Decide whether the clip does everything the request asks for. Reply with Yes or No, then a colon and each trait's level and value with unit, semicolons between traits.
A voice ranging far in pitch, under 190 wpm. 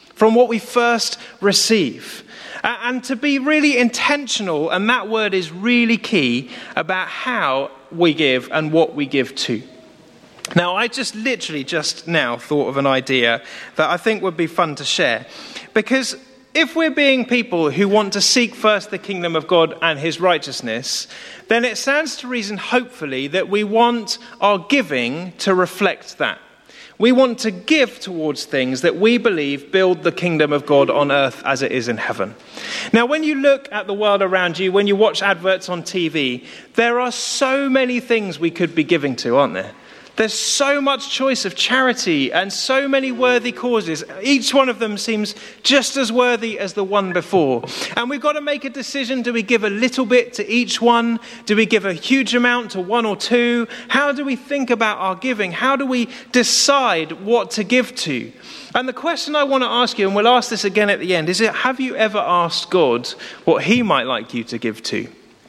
No: wide, 5.9 semitones; average, 200 wpm